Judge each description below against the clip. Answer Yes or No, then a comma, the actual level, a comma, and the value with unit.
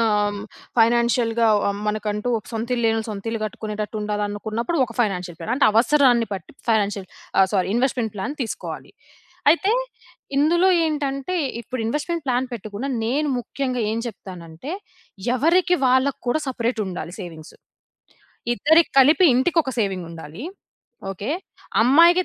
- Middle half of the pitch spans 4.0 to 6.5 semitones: Yes, average, 5.0 semitones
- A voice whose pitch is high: Yes, high, 230 Hz